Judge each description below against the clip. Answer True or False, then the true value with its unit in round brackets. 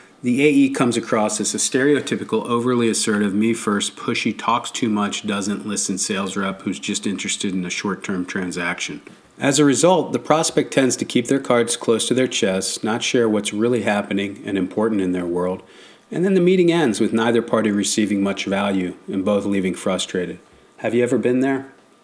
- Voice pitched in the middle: False (110 Hz)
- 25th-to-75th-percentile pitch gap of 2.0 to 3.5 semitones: False (3.9 semitones)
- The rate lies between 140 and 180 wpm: False (195 wpm)